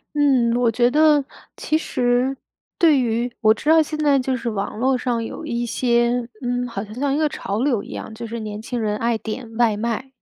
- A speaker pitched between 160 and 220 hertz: No, high, 245 Hz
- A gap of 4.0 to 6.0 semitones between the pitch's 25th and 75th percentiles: No, average, 2.8 semitones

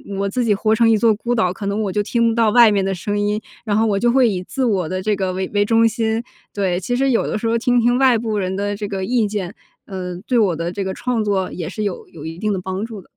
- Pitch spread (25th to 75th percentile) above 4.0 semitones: No, average, 3.1 semitones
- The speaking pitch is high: Yes, high, 210 Hz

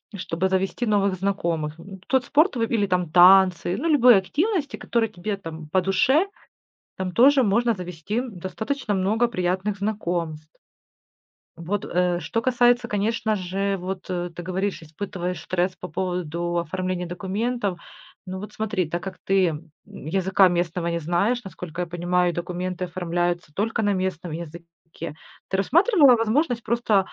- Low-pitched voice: No, high, 190 Hz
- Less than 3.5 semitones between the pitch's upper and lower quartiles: No, average, 3.8 semitones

